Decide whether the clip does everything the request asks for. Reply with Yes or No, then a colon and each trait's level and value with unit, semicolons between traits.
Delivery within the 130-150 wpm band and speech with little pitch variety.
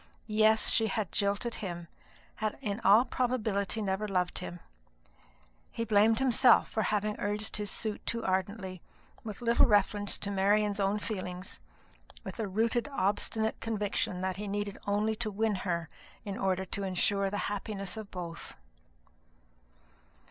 Yes: average, 145 wpm; narrow, 2.1 semitones